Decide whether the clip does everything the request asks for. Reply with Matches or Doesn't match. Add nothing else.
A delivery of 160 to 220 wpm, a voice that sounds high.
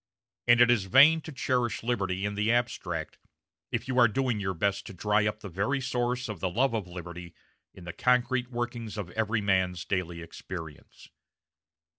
Doesn't match